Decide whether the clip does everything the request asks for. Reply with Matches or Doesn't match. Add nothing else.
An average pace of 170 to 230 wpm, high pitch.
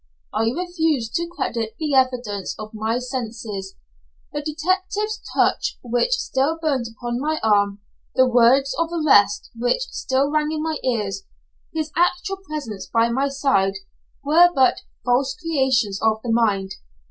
Doesn't match